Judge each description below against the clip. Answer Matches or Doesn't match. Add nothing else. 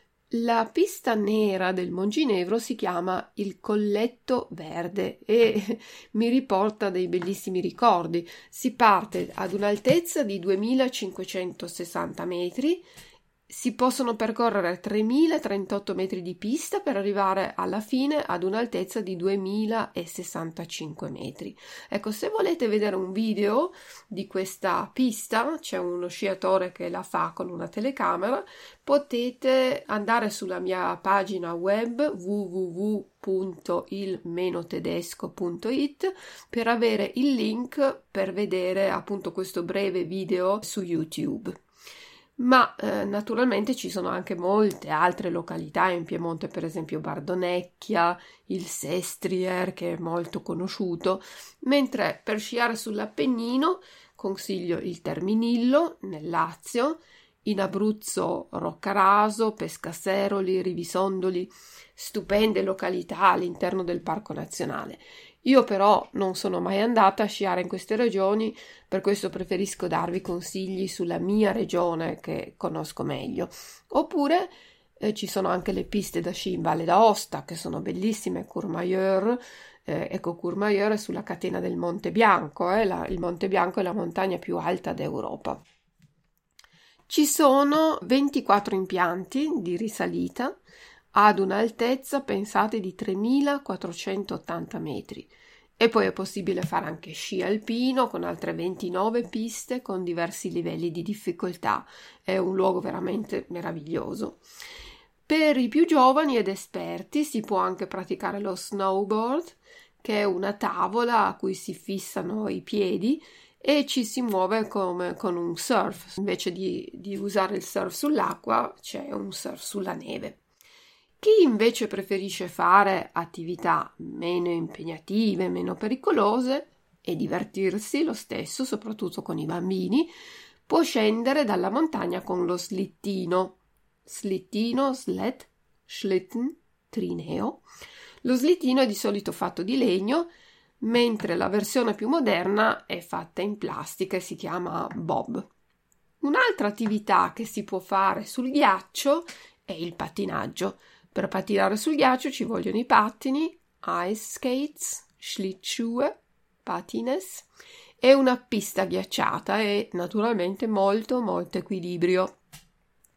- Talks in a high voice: Matches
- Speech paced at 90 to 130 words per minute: Matches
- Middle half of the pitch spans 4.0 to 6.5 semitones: Matches